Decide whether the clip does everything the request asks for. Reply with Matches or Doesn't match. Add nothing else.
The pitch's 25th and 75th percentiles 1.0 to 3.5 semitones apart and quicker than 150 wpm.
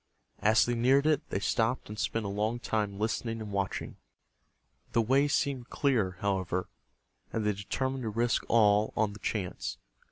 Matches